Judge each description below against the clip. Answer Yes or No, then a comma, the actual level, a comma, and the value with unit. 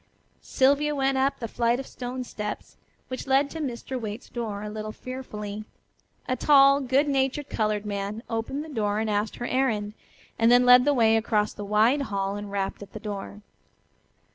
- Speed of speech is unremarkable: Yes, average, 185 wpm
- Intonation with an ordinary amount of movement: Yes, average, 4.1 semitones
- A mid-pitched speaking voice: No, high, 230 Hz